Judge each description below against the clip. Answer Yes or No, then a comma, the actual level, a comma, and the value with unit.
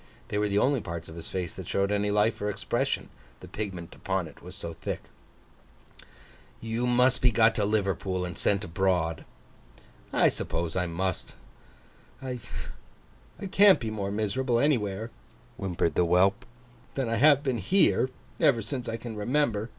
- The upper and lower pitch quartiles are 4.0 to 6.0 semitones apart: Yes, average, 4.4 semitones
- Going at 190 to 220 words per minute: No, average, 160 wpm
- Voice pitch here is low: Yes, low, 105 Hz